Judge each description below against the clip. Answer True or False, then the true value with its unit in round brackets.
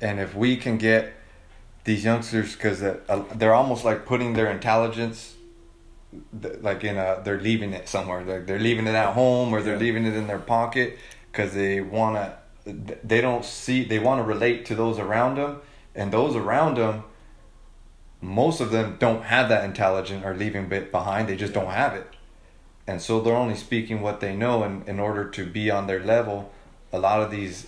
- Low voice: True (110 Hz)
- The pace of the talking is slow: False (190 wpm)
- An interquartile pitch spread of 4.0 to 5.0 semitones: False (2.7 semitones)